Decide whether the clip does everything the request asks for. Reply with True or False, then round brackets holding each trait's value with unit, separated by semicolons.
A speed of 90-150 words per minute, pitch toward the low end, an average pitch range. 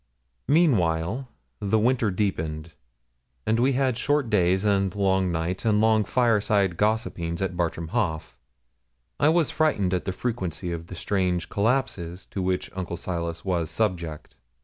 True (145 wpm; 95 Hz; 4.5 semitones)